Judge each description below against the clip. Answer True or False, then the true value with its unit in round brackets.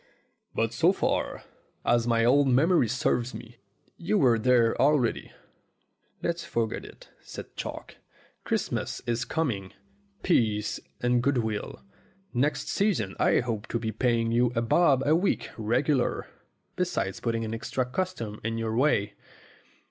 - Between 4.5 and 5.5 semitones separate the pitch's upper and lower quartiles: False (3.6 semitones)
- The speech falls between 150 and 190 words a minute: False (140 wpm)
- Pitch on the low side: True (120 Hz)